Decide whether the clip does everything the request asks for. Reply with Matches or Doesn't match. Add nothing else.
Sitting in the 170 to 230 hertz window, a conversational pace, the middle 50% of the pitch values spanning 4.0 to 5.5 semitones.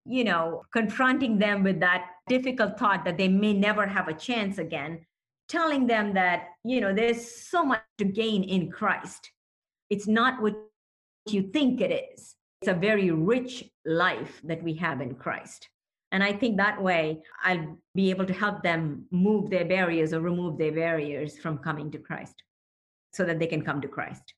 Matches